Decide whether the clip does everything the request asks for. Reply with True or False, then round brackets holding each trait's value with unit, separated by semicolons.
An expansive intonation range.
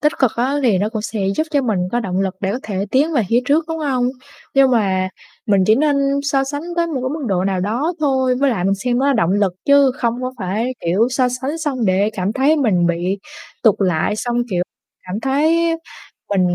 True (6.1 semitones)